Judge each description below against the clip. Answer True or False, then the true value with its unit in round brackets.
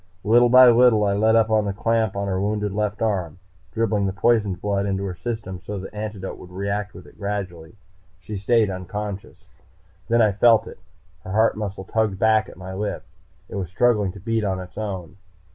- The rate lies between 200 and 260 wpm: True (205 wpm)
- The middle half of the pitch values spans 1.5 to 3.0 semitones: True (2.4 semitones)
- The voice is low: True (105 Hz)